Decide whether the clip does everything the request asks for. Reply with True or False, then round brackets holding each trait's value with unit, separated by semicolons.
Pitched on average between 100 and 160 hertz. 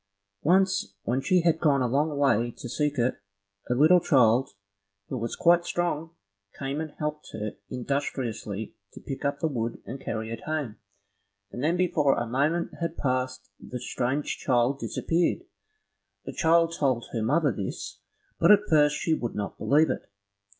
True (140 Hz)